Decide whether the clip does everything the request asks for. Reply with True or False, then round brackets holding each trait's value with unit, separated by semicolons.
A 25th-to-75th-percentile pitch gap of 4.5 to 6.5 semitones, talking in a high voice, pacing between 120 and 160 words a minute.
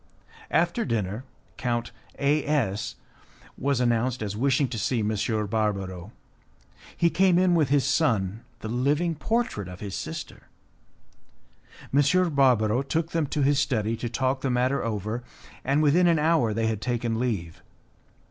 False (5.1 semitones; 125 Hz; 145 wpm)